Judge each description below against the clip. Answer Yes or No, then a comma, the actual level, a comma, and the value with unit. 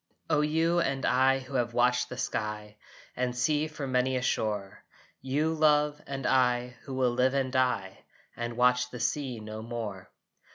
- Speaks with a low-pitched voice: Yes, low, 125 Hz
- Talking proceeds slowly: No, average, 170 wpm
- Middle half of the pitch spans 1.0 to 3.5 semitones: Yes, narrow, 2.4 semitones